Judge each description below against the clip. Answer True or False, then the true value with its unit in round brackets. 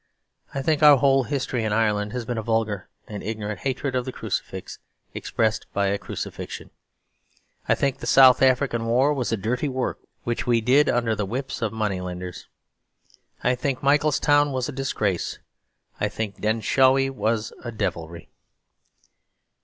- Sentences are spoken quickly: False (155 wpm)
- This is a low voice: True (120 Hz)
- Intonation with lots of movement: False (3.8 semitones)